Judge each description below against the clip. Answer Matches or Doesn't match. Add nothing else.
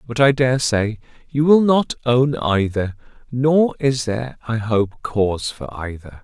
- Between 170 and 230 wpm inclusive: Doesn't match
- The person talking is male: Matches